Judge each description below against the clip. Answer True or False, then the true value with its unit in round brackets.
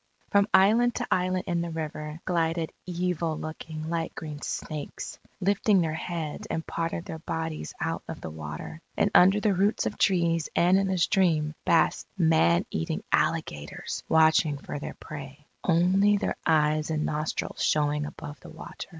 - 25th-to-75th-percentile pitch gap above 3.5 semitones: False (3.0 semitones)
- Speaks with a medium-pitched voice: True (160 Hz)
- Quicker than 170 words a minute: False (165 wpm)